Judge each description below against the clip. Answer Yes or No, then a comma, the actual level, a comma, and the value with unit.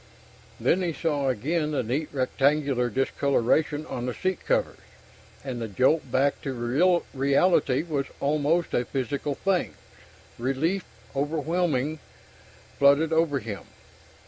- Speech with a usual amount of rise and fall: Yes, average, 3.6 semitones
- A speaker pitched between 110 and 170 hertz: Yes, medium, 140 Hz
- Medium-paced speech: No, slow, 120 wpm